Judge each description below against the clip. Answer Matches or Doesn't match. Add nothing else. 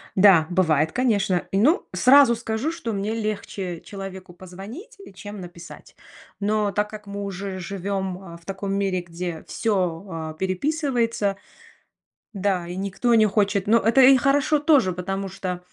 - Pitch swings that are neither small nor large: Matches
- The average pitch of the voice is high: Matches